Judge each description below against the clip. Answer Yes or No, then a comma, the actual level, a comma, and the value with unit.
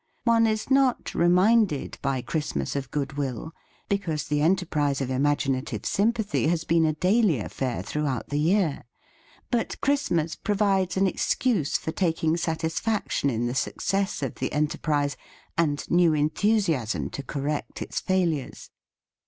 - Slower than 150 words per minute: Yes, slow, 135 wpm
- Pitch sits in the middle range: Yes, medium, 160 Hz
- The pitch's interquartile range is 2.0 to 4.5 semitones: No, wide, 5.6 semitones